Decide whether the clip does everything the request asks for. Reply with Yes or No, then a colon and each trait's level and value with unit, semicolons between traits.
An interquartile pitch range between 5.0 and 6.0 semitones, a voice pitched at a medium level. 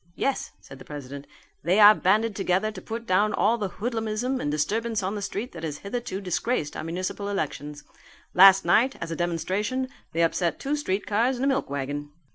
No: wide, 5.4 semitones; high, 200 Hz